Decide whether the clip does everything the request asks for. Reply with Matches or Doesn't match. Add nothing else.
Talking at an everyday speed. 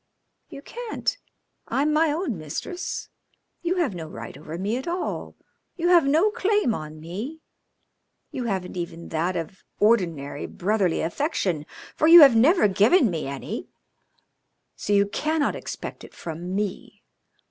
Matches